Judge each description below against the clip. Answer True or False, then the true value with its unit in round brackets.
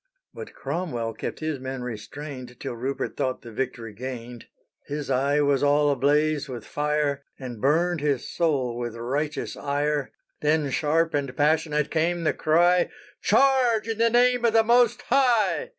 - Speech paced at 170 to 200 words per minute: False (155 wpm)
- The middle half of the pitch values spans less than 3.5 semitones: False (4.5 semitones)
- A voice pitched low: False (145 Hz)